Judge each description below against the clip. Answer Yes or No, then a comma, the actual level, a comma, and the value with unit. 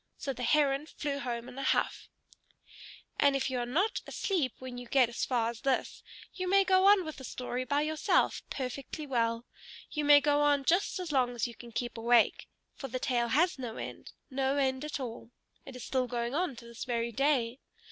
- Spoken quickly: Yes, fast, 210 wpm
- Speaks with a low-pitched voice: No, very high, 265 Hz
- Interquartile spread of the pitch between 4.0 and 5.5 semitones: No, average, 3.3 semitones